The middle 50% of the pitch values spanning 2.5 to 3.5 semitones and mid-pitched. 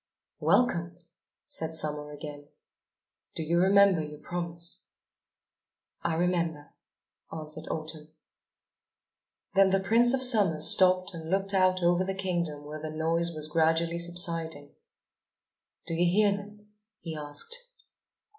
Yes: average, 3.2 semitones; medium, 170 Hz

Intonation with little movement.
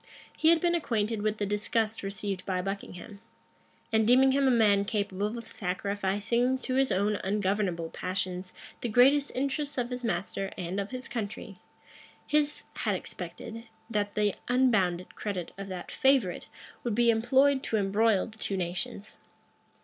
No: average, 4.0 semitones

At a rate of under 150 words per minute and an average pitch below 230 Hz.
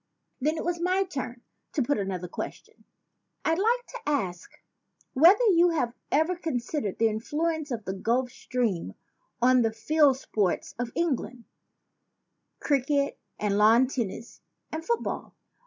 No: average, 140 wpm; very high, 265 Hz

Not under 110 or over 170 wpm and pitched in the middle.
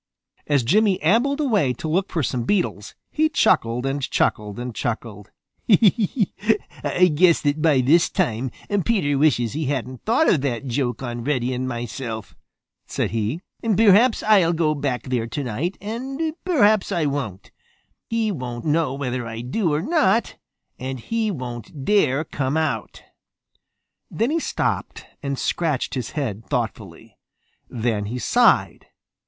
Yes: average, 145 wpm; medium, 145 Hz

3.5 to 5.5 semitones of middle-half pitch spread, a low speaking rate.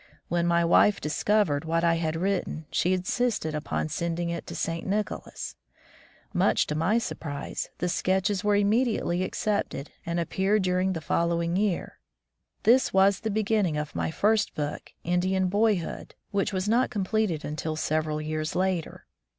No: average, 3.9 semitones; average, 155 wpm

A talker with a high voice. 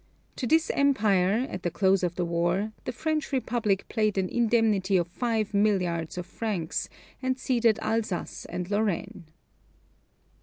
Yes: high, 205 Hz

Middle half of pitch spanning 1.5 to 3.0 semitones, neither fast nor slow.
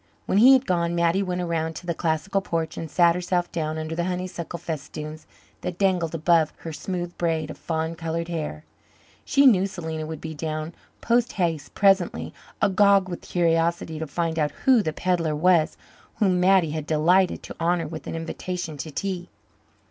Yes: narrow, 2.4 semitones; average, 175 wpm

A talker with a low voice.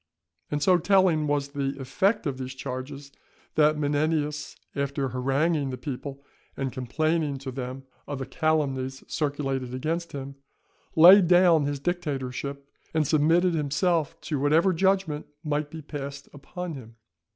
No: medium, 145 Hz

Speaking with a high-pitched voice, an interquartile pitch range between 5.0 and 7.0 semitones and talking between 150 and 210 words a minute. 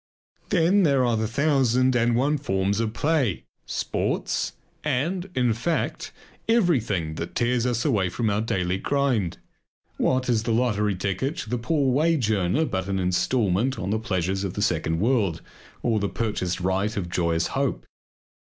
No: low, 115 Hz; wide, 5.5 semitones; average, 160 wpm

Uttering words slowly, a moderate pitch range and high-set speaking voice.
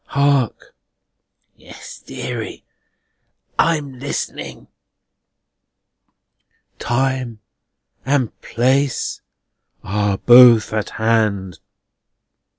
No: slow, 55 wpm; average, 3.7 semitones; low, 120 Hz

